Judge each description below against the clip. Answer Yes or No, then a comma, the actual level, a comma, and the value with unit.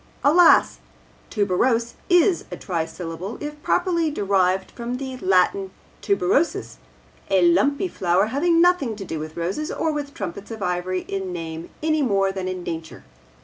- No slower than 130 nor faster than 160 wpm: Yes, average, 145 wpm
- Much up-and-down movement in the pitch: Yes, wide, 8.0 semitones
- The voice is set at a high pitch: Yes, high, 200 Hz